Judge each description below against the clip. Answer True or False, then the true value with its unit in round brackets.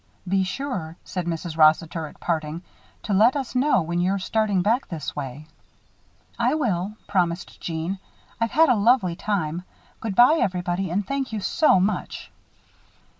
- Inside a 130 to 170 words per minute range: True (155 wpm)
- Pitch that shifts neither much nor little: True (5.0 semitones)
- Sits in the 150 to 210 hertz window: True (190 Hz)